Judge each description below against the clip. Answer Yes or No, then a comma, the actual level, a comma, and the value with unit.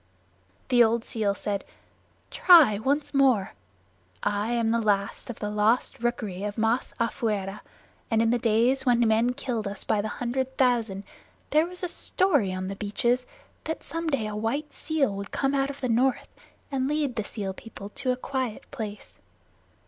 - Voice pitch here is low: No, high, 235 Hz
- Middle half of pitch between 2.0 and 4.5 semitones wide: Yes, average, 4.0 semitones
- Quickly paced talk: No, average, 170 wpm